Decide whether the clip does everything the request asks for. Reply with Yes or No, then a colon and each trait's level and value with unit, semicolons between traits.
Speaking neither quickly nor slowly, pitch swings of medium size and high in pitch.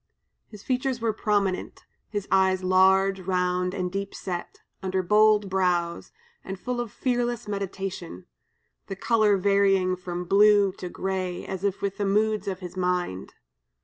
No: average, 145 wpm; narrow, 2.2 semitones; high, 195 Hz